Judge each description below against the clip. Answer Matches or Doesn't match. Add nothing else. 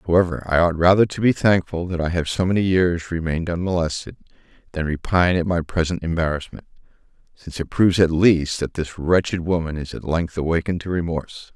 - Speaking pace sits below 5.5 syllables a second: Doesn't match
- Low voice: Matches